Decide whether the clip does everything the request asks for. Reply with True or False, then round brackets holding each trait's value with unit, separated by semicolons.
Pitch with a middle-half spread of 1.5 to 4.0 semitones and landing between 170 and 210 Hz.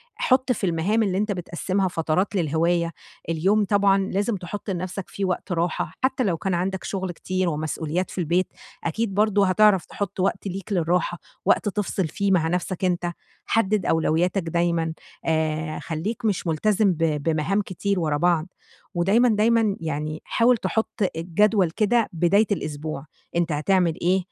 True (3.5 semitones; 185 Hz)